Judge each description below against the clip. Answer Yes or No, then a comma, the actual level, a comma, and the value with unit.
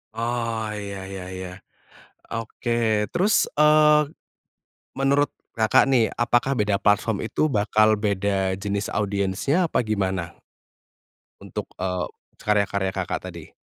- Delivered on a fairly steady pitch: No, average, 3.4 semitones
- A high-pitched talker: No, low, 105 Hz